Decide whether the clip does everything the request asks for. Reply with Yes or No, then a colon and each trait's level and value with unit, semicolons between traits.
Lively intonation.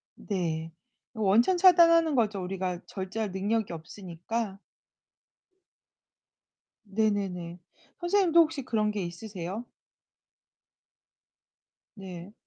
No: average, 4.2 semitones